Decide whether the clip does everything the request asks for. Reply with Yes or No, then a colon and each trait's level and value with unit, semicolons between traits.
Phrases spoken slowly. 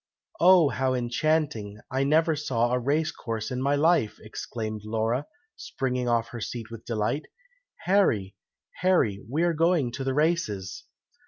No: average, 150 wpm